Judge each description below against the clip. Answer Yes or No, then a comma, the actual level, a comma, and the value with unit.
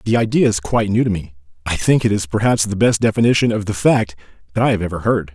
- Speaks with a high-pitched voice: No, low, 105 Hz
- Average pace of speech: No, fast, 245 wpm